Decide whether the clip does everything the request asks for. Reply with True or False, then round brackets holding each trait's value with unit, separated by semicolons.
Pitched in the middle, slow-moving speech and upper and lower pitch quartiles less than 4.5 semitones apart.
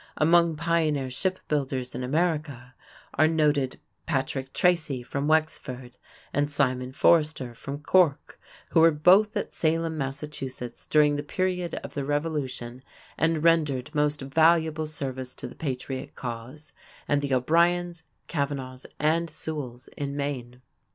True (145 Hz; 130 wpm; 3.4 semitones)